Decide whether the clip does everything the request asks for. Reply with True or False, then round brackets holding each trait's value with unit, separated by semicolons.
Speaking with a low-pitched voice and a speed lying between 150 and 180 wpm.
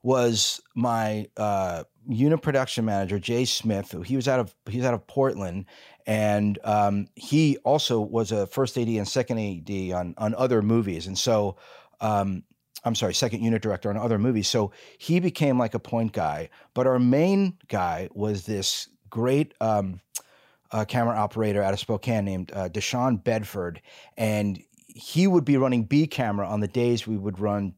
True (110 Hz; 175 wpm)